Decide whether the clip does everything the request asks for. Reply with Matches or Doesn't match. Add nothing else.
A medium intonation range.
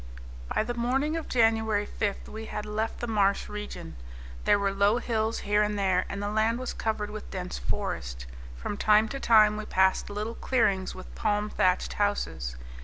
Doesn't match